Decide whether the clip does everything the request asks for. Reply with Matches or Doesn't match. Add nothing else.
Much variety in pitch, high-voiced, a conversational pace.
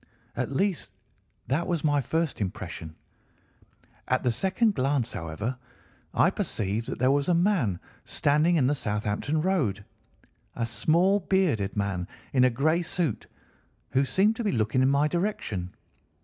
Doesn't match